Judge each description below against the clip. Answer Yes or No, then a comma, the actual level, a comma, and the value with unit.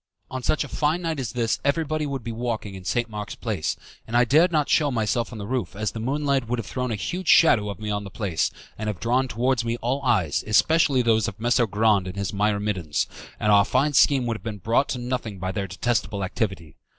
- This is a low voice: Yes, low, 115 Hz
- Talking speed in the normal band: No, fast, 235 wpm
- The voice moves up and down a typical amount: Yes, average, 4.1 semitones